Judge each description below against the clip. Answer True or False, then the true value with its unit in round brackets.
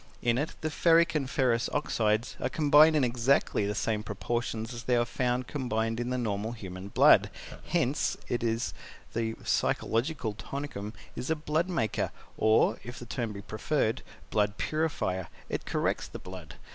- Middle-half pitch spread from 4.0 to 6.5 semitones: True (4.3 semitones)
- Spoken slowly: False (170 wpm)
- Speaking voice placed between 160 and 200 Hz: False (120 Hz)